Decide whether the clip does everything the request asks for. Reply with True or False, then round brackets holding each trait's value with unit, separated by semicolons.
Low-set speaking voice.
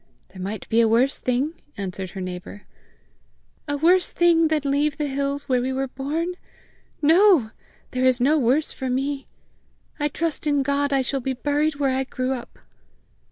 False (275 Hz)